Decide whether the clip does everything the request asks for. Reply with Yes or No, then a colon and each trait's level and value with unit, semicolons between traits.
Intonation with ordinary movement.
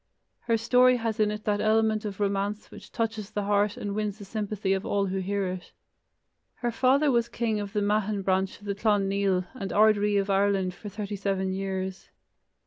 No: narrow, 1.8 semitones